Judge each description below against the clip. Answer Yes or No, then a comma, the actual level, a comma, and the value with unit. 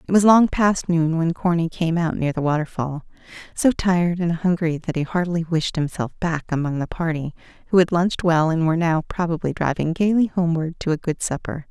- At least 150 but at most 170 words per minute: No, fast, 205 wpm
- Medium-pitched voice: Yes, medium, 170 Hz